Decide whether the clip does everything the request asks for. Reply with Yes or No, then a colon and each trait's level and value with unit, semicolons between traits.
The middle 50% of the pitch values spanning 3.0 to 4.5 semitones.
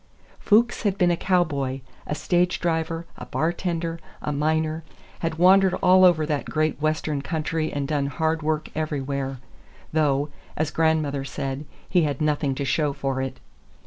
No: narrow, 2.6 semitones